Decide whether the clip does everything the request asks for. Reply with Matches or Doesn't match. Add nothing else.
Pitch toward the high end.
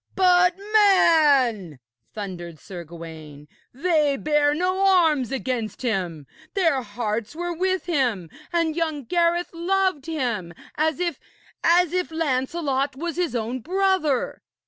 Matches